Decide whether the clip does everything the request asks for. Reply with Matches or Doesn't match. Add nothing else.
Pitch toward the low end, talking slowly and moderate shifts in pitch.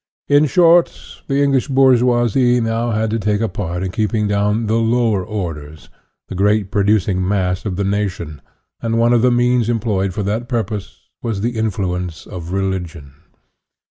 Doesn't match